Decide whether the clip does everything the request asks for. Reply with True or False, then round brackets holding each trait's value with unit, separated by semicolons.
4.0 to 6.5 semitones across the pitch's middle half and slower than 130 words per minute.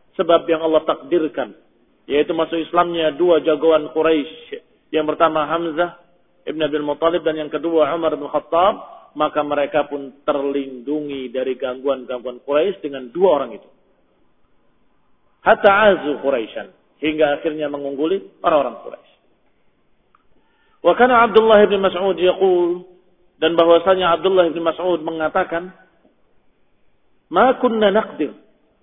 False (3.2 semitones; 115 wpm)